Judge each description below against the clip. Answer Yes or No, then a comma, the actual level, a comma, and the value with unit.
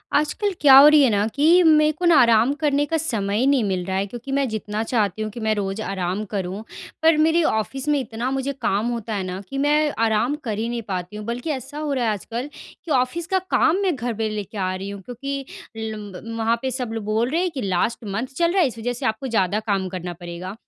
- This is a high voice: Yes, high, 230 Hz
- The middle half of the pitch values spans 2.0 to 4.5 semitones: No, average, 5.2 semitones